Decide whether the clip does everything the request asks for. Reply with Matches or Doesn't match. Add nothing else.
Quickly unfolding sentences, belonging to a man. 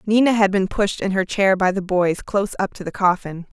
Doesn't match